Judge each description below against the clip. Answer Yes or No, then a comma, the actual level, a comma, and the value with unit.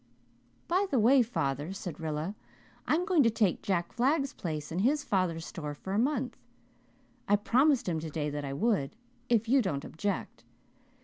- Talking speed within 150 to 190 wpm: Yes, average, 170 wpm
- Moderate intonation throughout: No, wide, 8.0 semitones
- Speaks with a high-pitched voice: Yes, high, 200 Hz